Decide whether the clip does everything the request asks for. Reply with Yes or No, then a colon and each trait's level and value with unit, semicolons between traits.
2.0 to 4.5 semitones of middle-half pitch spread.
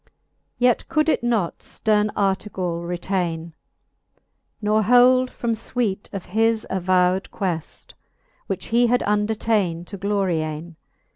Yes: average, 4.2 semitones